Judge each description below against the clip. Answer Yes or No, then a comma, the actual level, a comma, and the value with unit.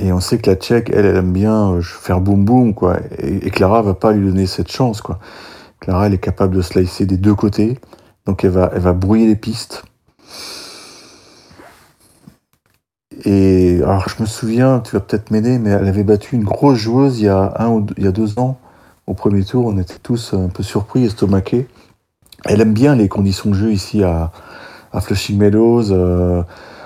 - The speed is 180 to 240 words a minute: Yes, average, 205 wpm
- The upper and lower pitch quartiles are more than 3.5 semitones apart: No, average, 3.0 semitones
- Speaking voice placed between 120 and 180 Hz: No, low, 100 Hz